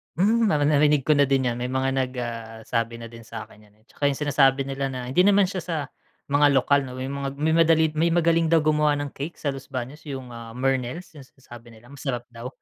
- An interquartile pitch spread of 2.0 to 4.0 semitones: Yes, average, 3.7 semitones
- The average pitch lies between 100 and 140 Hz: Yes, low, 135 Hz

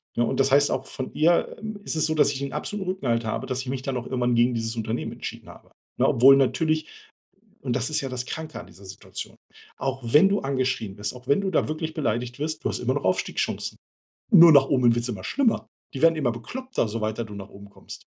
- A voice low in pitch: Yes, low, 130 Hz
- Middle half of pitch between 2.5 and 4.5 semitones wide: No, average, 4.9 semitones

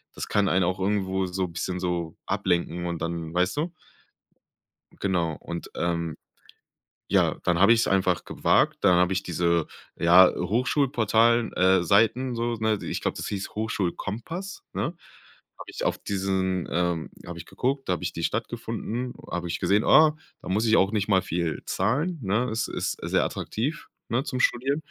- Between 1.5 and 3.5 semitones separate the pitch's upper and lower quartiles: No, average, 4.7 semitones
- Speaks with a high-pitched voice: No, very low, 95 Hz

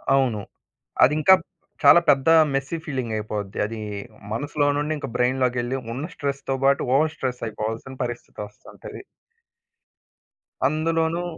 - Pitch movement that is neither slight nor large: Yes, average, 3.4 semitones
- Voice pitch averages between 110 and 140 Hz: Yes, low, 135 Hz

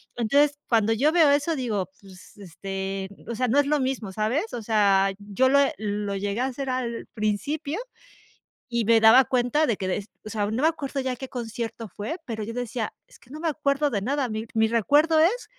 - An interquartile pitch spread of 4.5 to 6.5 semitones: Yes, average, 5.0 semitones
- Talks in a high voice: Yes, high, 235 Hz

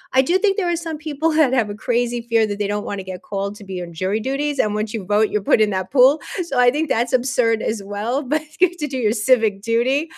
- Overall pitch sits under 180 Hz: No, high, 235 Hz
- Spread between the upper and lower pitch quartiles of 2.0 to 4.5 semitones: No, average, 5.3 semitones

